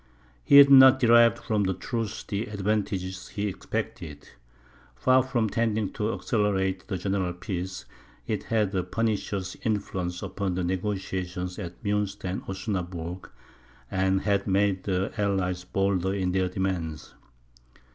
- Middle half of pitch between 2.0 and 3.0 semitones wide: Yes, narrow, 2.4 semitones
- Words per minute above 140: No, slow, 135 wpm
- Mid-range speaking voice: No, very low, 95 Hz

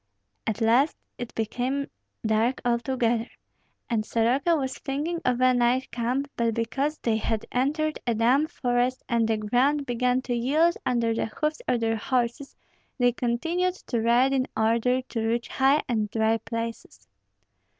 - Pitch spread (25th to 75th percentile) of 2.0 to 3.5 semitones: Yes, average, 2.7 semitones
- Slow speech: No, average, 155 wpm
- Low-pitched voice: No, high, 245 Hz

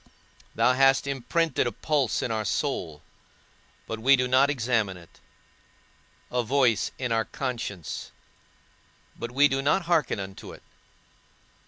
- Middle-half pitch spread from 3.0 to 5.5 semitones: Yes, average, 3.8 semitones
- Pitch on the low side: Yes, low, 125 Hz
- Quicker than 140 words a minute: No, slow, 135 wpm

